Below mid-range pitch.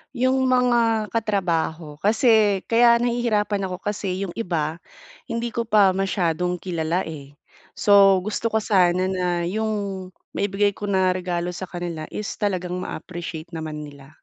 No: high, 190 Hz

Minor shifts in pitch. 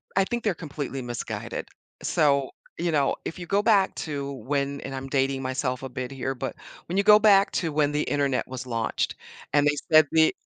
No: average, 3.8 semitones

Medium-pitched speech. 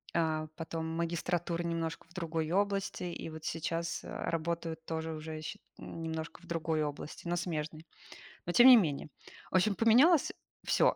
Yes: medium, 165 Hz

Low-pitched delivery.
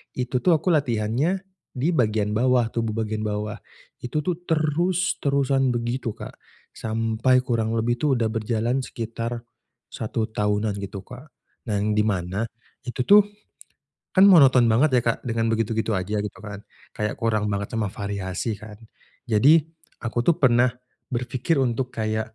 Yes: low, 115 Hz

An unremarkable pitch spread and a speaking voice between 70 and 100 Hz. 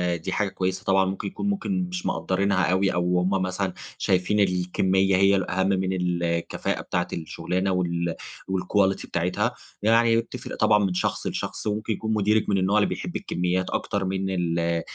No: narrow, 1.9 semitones; very low, 95 Hz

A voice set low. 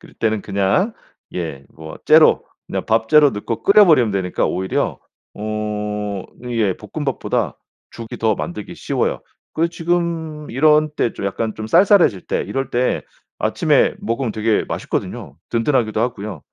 Yes: low, 115 Hz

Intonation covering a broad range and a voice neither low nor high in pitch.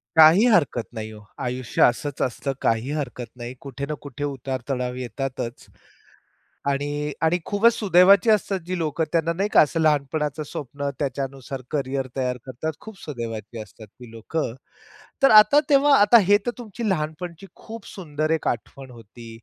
Yes: wide, 5.9 semitones; medium, 145 Hz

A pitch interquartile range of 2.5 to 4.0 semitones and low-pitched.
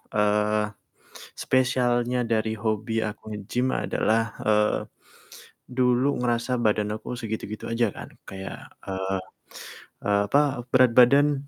Yes: average, 2.9 semitones; low, 115 Hz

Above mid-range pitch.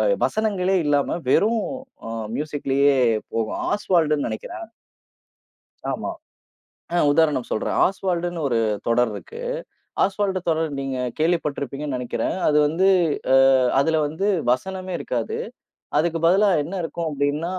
No: medium, 155 Hz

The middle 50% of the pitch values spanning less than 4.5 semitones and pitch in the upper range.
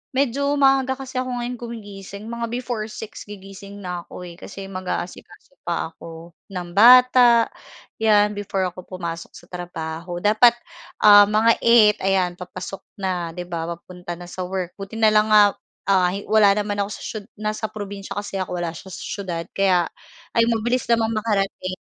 Yes: average, 3.8 semitones; high, 200 Hz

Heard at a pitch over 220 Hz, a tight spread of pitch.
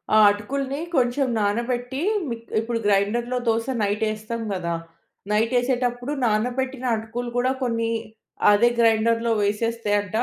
Yes: high, 230 Hz; narrow, 2.3 semitones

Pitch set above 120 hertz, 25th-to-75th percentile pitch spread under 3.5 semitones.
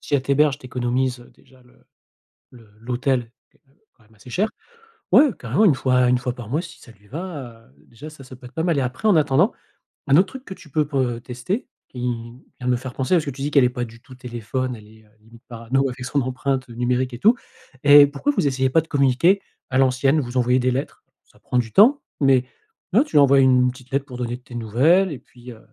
Yes: low, 130 Hz; average, 2.8 semitones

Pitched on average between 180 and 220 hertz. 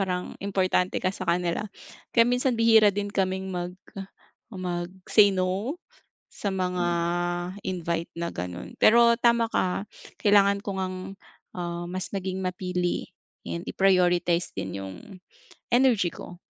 Yes: medium, 185 Hz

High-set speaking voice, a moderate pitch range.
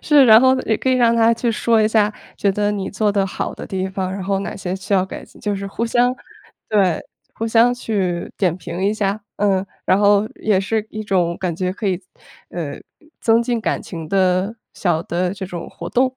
Yes: high, 200 Hz; average, 3.2 semitones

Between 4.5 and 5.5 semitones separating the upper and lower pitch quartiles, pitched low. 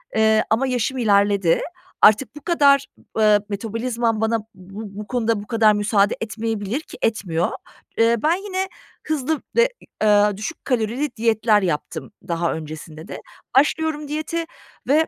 No: average, 5.0 semitones; high, 225 Hz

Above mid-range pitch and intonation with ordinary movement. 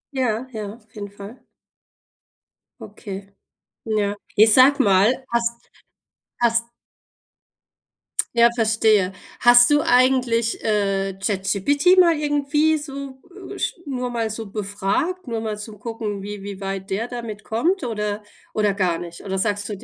Yes: high, 220 Hz; average, 3.7 semitones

